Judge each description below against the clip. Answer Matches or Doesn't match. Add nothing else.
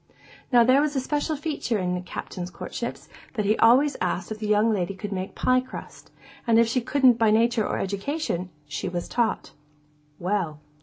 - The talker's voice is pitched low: Doesn't match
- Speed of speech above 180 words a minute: Matches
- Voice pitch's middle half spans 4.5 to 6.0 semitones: Matches